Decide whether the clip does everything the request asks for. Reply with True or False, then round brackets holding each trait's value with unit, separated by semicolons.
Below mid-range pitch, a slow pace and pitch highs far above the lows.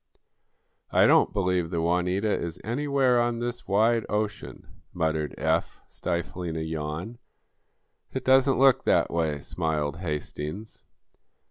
True (90 Hz; 125 wpm; 6.6 semitones)